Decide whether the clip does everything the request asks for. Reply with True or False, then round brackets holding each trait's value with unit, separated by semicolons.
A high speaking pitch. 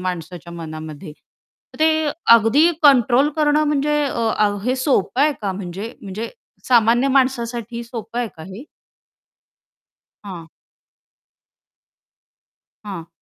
True (230 Hz)